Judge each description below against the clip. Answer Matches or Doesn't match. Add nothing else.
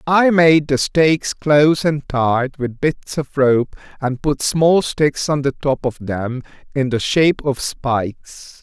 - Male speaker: Matches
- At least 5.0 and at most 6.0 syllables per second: Doesn't match